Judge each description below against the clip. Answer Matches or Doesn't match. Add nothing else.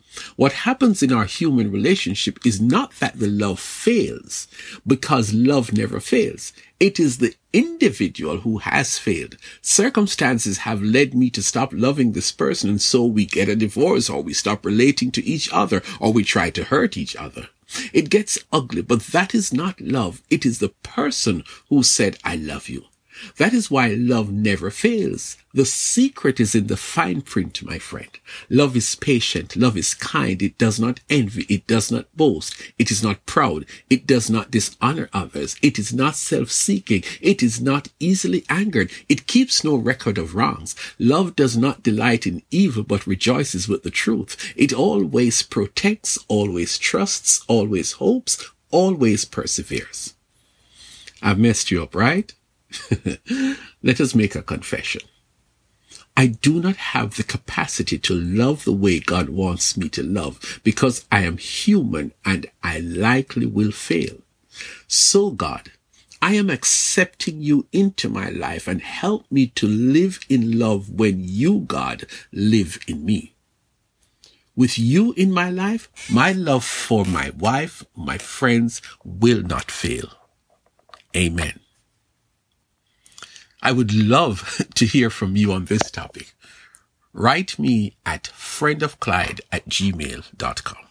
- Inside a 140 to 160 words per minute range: Matches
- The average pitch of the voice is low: Matches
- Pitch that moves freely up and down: Matches